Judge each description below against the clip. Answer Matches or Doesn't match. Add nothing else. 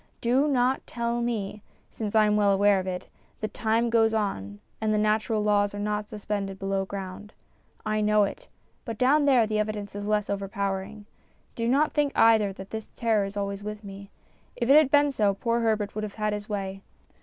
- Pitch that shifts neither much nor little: Doesn't match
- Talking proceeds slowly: Doesn't match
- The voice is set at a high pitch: Matches